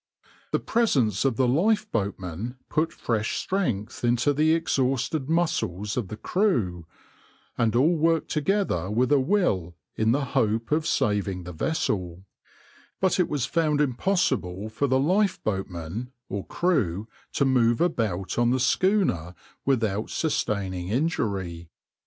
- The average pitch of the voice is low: Yes, low, 120 Hz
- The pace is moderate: No, slow, 130 wpm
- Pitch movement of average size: No, wide, 7.8 semitones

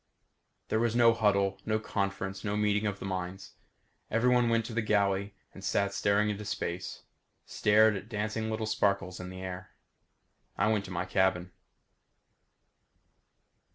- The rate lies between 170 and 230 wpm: No, average, 155 wpm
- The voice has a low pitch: Yes, low, 100 Hz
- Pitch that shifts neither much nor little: No, narrow, 2.2 semitones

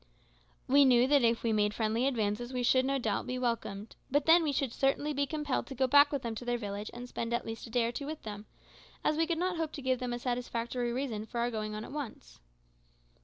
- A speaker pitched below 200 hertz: No, high, 245 Hz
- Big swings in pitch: No, average, 3.5 semitones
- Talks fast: Yes, fast, 255 wpm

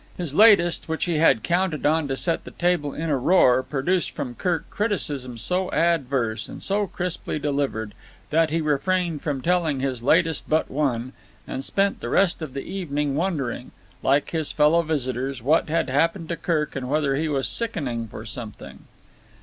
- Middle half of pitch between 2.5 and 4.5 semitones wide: Yes, average, 4.2 semitones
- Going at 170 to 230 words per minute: Yes, average, 175 wpm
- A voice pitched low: No, medium, 150 Hz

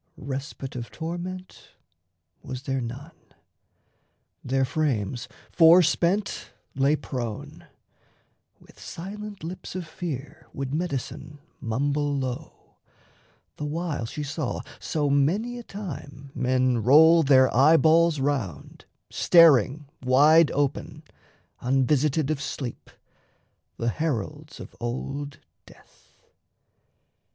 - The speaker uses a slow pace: Yes, slow, 95 wpm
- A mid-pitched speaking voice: Yes, medium, 145 Hz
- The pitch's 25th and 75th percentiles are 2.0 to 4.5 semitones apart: Yes, average, 3.8 semitones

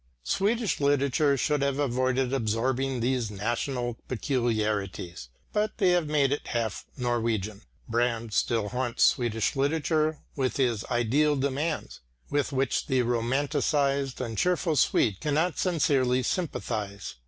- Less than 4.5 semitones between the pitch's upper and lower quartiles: Yes, average, 3.8 semitones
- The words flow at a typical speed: No, slow, 120 wpm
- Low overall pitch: Yes, low, 130 Hz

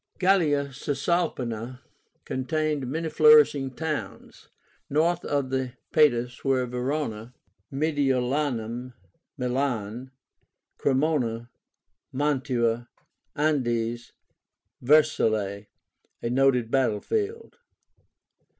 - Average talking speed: No, slow, 75 wpm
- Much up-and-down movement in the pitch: No, average, 3.9 semitones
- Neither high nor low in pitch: No, low, 130 Hz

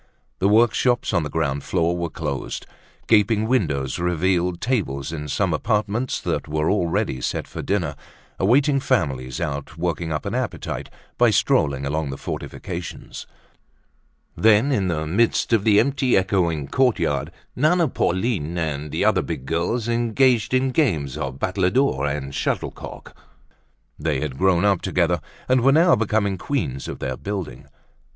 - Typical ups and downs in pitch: No, wide, 7.2 semitones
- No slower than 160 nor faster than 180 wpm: No, average, 145 wpm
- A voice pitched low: Yes, very low, 90 Hz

